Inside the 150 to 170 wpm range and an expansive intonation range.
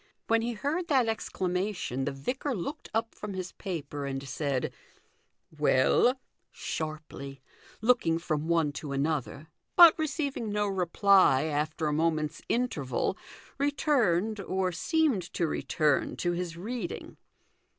No: slow, 135 wpm; wide, 7.0 semitones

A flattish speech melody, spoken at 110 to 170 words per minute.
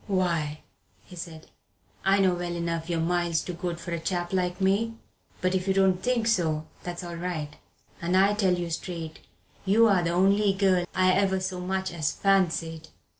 No: narrow, 2.1 semitones; average, 180 wpm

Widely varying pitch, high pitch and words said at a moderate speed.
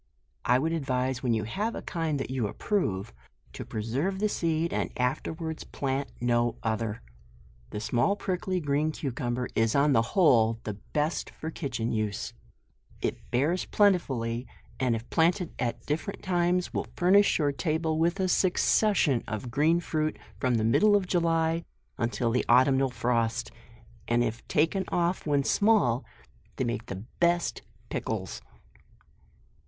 No: wide, 6.3 semitones; medium, 140 Hz; average, 150 wpm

